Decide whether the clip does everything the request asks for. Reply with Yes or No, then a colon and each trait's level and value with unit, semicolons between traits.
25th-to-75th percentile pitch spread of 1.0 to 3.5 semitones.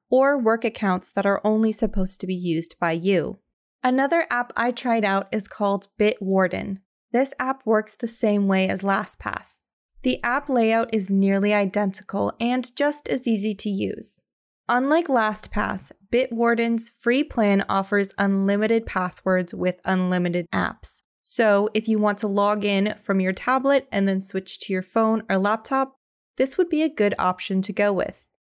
Yes: average, 3.2 semitones